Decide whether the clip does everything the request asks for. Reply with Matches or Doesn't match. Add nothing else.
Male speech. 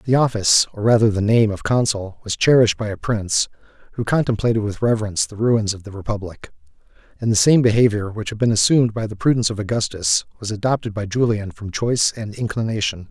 Matches